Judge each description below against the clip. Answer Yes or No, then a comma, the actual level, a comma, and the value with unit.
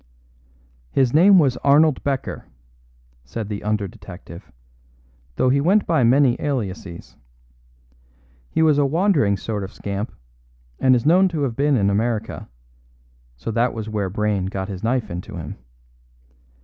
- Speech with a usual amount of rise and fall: No, wide, 6.1 semitones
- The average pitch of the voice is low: Yes, low, 120 Hz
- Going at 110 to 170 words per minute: Yes, average, 145 wpm